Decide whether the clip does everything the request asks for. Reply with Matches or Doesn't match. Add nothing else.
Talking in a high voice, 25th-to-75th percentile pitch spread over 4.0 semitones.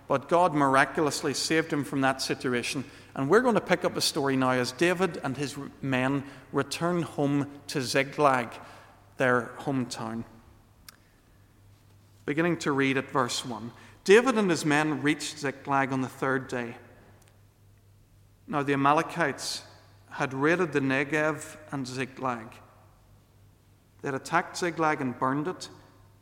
Doesn't match